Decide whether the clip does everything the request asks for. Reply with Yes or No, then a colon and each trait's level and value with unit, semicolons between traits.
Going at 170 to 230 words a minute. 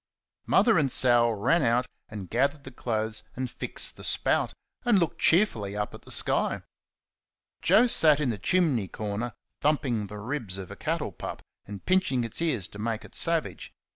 Yes: average, 175 wpm